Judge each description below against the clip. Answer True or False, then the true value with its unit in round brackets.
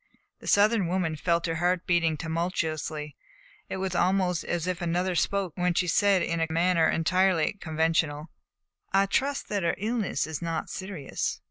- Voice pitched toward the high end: False (175 Hz)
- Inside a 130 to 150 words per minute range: False (165 wpm)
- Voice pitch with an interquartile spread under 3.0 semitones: True (2.5 semitones)